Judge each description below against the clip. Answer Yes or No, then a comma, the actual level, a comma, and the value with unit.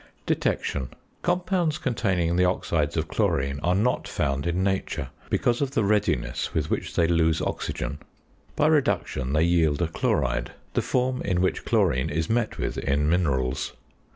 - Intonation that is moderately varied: No, wide, 7.1 semitones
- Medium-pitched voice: No, very low, 85 Hz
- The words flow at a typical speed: Yes, average, 155 wpm